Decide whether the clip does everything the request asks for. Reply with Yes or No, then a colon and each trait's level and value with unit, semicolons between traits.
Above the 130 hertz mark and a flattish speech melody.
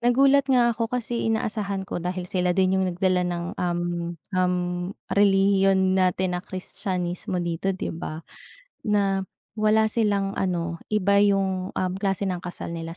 Yes: high, 190 Hz; narrow, 2.2 semitones